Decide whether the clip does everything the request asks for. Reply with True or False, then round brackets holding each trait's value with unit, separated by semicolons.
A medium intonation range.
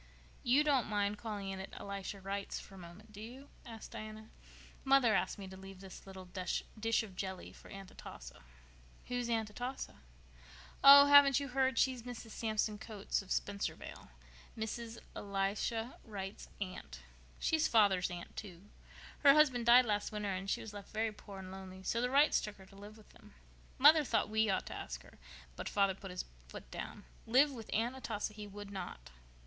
True (3.5 semitones)